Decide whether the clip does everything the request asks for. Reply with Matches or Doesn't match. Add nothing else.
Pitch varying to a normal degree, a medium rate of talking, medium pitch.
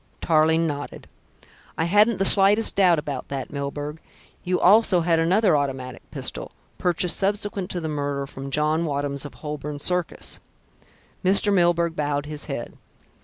Matches